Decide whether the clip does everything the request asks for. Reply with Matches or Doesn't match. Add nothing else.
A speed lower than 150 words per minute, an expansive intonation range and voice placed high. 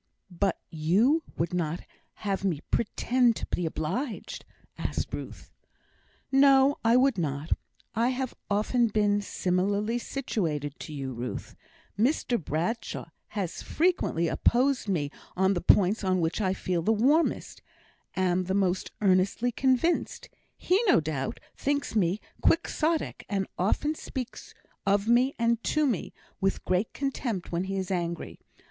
Matches